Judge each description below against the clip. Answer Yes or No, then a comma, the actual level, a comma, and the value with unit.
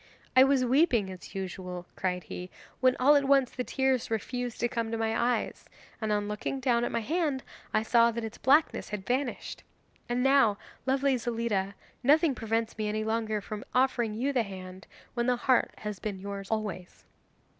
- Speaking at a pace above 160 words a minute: Yes, average, 185 wpm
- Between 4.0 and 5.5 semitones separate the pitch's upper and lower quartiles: No, average, 3.6 semitones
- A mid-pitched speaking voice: No, high, 230 Hz